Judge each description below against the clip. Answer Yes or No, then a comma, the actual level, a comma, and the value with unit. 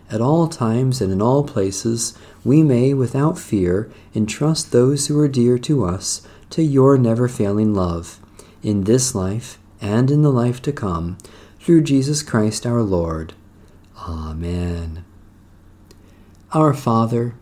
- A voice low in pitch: Yes, low, 110 Hz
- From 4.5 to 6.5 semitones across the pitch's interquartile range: Yes, average, 4.9 semitones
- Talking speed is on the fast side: No, average, 140 wpm